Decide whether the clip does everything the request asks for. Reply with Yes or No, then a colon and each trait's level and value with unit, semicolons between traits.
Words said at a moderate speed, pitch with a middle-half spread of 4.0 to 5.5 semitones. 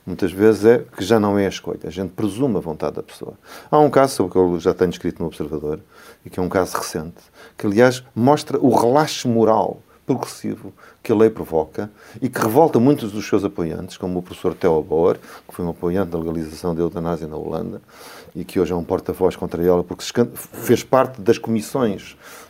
No: fast, 215 wpm; average, 4.7 semitones